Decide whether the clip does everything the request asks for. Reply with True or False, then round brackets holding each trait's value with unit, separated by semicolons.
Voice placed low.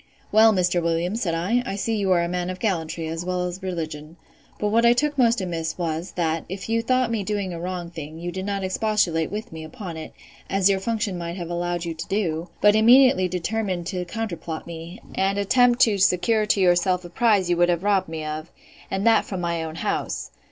False (185 Hz)